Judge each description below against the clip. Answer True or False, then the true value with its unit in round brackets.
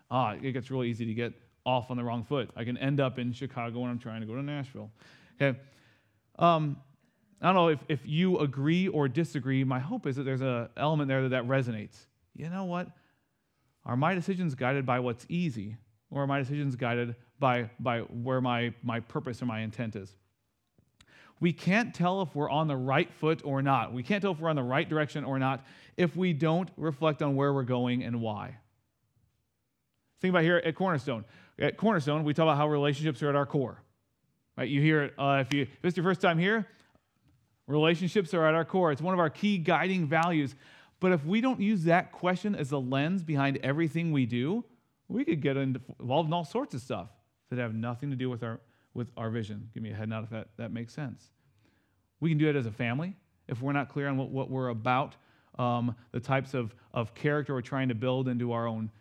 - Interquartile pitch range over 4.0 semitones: True (4.7 semitones)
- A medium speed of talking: False (220 wpm)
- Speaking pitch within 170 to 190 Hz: False (135 Hz)